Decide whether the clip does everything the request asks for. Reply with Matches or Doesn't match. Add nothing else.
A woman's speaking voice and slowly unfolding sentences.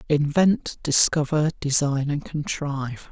Doesn't match